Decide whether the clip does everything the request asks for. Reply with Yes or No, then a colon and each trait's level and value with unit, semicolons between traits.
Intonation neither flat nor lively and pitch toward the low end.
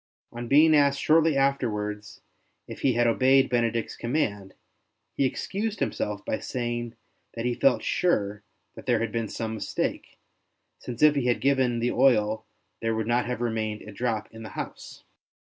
Yes: average, 3.5 semitones; low, 120 Hz